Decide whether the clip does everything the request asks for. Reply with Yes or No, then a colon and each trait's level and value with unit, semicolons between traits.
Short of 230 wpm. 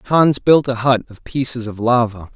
Yes: fast, 205 wpm